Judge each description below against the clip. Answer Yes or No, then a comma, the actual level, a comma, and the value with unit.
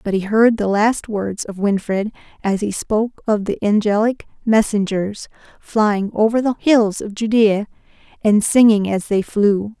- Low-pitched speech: No, high, 210 Hz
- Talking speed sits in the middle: Yes, average, 160 wpm